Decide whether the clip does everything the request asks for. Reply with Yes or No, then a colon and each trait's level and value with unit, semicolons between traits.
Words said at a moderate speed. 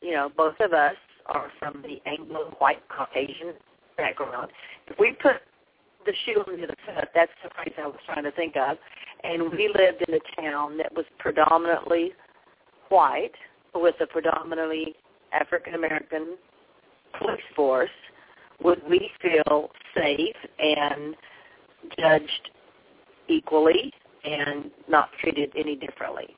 No: slow, 130 wpm